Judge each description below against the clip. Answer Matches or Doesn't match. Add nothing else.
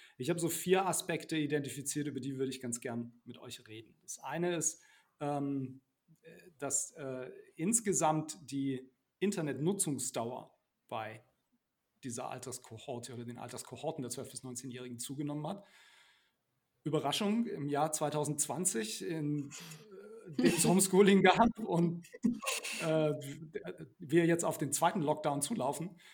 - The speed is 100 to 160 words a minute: Matches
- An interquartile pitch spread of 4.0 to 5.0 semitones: Matches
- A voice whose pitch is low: Doesn't match